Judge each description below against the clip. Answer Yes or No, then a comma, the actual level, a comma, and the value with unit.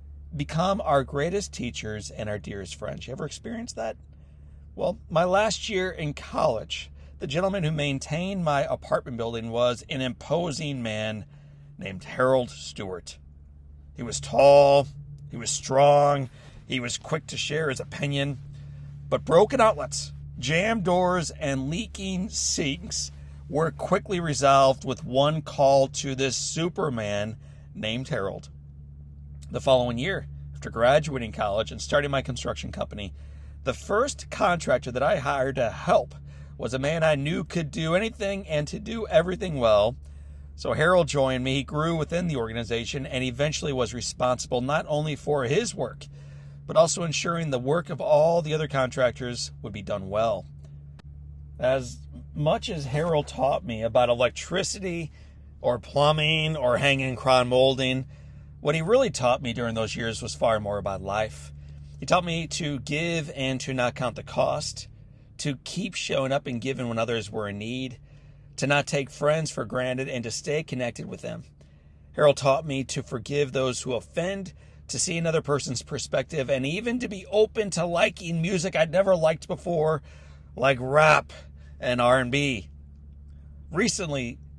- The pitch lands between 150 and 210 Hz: No, low, 135 Hz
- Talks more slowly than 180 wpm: Yes, average, 155 wpm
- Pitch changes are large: Yes, wide, 6.3 semitones